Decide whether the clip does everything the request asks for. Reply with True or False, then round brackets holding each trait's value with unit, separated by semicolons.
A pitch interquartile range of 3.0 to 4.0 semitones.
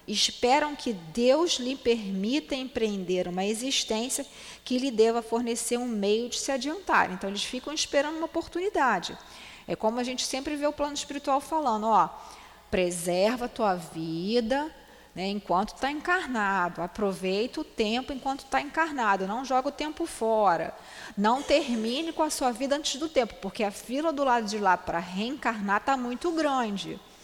False (5.5 semitones)